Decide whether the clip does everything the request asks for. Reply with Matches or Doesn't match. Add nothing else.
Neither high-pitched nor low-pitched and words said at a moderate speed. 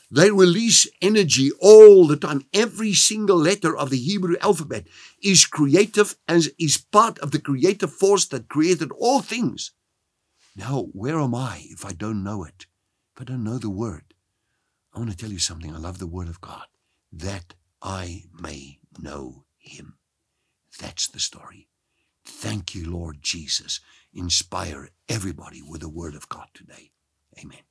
Doesn't match